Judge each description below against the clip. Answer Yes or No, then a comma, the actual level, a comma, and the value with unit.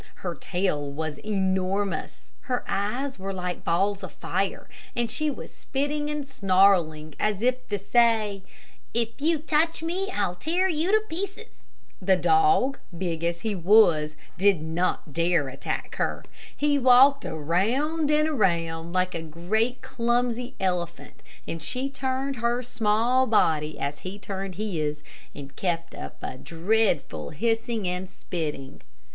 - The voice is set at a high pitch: Yes, high, 205 Hz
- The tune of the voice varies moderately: No, wide, 7.2 semitones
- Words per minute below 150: Yes, average, 140 wpm